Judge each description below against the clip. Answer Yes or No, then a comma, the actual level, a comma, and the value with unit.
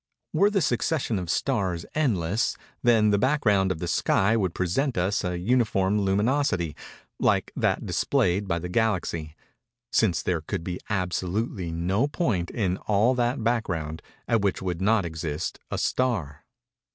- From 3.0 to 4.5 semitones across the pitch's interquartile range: No, average, 5.1 semitones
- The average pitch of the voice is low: Yes, low, 100 Hz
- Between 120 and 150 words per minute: Yes, average, 145 wpm